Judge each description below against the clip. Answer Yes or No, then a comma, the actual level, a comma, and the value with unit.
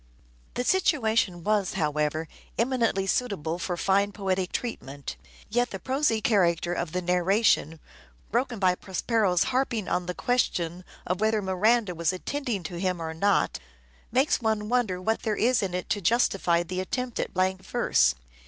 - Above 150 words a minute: Yes, average, 160 wpm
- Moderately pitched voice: No, high, 195 Hz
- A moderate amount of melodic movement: Yes, average, 4.4 semitones